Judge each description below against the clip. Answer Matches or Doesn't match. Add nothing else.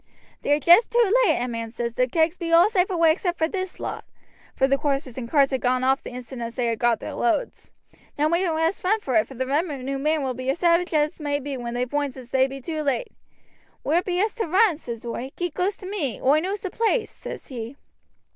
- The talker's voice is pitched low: Doesn't match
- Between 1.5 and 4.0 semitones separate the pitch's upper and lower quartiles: Doesn't match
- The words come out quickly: Matches